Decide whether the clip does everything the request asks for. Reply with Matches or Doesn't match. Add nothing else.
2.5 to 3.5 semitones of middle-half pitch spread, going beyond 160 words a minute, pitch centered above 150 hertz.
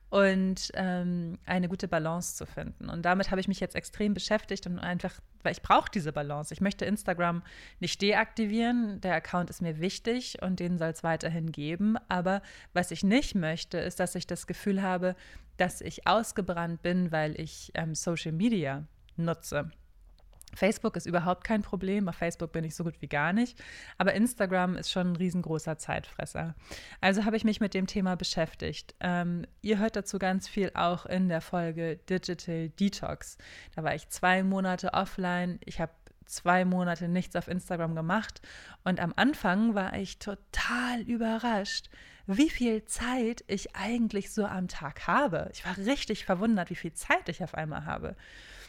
Matches